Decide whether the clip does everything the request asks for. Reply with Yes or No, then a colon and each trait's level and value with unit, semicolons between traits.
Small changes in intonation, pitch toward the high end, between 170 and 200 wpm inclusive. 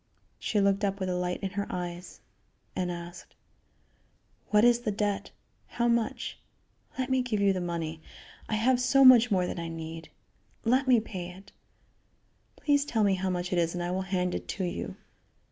No: average, 4.5 semitones; high, 195 Hz; average, 190 wpm